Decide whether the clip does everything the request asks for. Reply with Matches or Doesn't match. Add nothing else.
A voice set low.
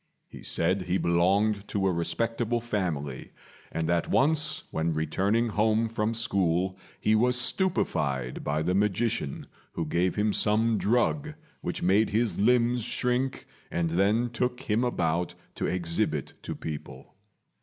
Matches